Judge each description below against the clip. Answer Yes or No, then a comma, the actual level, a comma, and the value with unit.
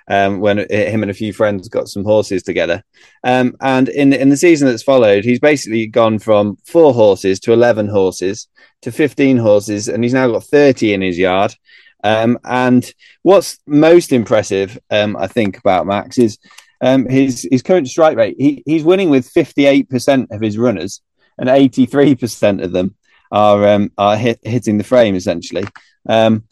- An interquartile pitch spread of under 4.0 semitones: No, average, 4.5 semitones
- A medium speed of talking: Yes, average, 175 wpm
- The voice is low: Yes, low, 120 Hz